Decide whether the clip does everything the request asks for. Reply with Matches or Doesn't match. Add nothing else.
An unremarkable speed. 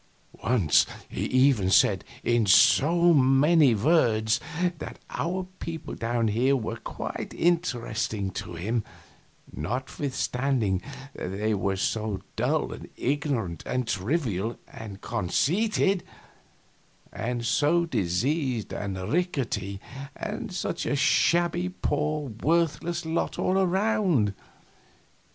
Doesn't match